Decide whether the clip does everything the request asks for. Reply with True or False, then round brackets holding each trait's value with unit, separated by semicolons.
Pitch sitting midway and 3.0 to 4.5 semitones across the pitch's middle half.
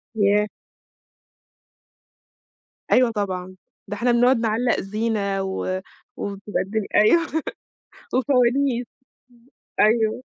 False (220 Hz; 3.5 semitones)